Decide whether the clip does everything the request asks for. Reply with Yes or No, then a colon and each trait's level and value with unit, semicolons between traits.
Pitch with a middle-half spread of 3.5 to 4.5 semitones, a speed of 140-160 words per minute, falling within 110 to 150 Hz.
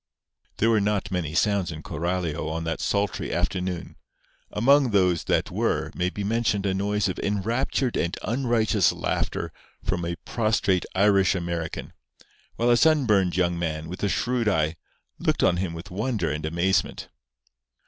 No: average, 3.8 semitones; average, 155 wpm; very low, 95 Hz